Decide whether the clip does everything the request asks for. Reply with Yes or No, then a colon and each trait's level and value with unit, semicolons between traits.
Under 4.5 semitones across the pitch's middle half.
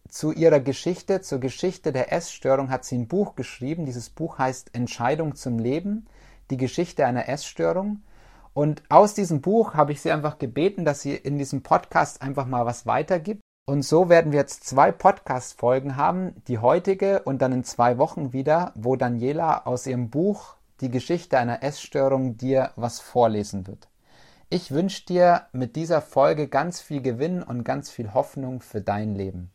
No: average, 4.9 semitones